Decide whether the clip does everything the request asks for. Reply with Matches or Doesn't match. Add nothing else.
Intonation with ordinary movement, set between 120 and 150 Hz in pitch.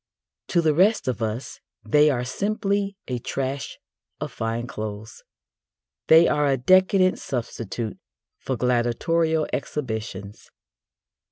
Doesn't match